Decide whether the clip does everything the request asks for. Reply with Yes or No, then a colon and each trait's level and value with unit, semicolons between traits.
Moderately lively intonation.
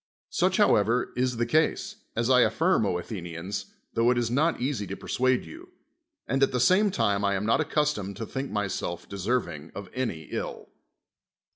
Yes: average, 4.9 semitones